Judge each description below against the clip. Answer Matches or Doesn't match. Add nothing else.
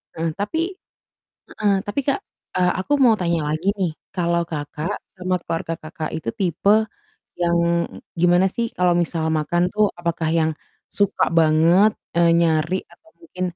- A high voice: Doesn't match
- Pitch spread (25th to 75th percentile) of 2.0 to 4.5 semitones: Matches